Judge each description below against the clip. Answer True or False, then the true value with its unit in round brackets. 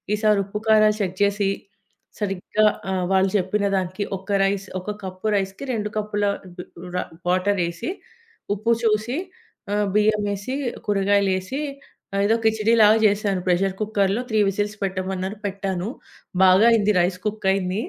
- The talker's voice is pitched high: True (200 Hz)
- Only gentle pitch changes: True (1.9 semitones)